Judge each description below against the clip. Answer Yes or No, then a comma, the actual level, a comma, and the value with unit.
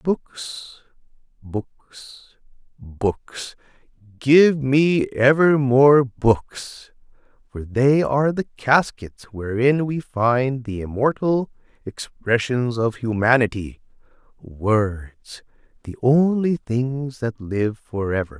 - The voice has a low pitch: Yes, low, 125 Hz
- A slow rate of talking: Yes, slow, 85 wpm